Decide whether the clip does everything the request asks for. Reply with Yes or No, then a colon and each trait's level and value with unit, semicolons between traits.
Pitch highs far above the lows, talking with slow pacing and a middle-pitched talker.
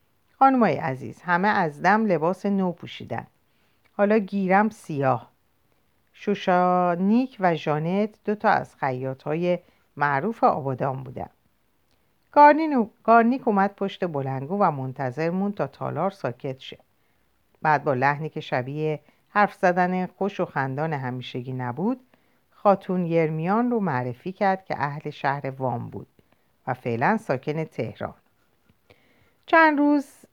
No: wide, 6.3 semitones; average, 120 wpm; medium, 180 Hz